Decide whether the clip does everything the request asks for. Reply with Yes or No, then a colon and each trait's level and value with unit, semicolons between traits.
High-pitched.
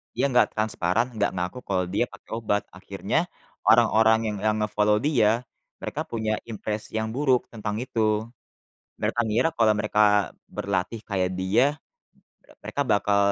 No: low, 105 Hz